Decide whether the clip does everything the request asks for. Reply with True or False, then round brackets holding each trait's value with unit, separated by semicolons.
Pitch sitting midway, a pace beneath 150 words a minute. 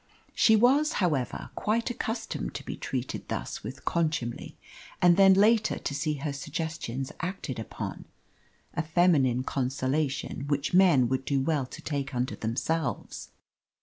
True (150 Hz; 140 wpm)